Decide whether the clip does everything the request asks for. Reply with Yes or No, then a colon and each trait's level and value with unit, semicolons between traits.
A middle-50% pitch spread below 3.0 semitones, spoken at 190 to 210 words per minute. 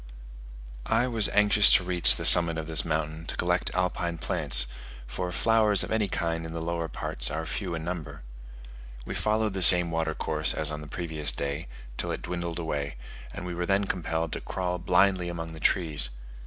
Yes: narrow, 2.4 semitones; average, 195 wpm